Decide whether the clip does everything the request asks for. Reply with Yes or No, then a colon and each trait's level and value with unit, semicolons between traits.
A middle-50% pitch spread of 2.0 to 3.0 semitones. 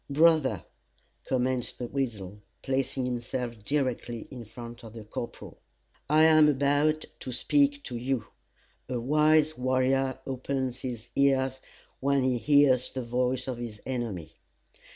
Yes: average, 2.7 semitones